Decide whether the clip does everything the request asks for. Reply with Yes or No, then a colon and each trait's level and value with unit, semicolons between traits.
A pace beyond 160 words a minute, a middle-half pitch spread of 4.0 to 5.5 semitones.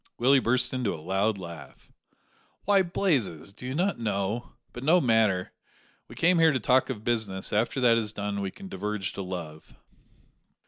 Yes: average, 175 wpm; average, 5.0 semitones